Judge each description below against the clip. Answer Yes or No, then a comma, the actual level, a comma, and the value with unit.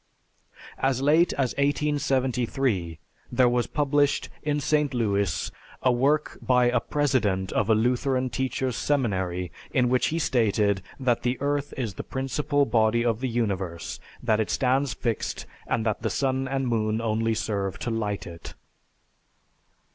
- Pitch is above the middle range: No, low, 125 Hz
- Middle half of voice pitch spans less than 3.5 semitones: No, average, 3.8 semitones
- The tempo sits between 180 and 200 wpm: No, average, 145 wpm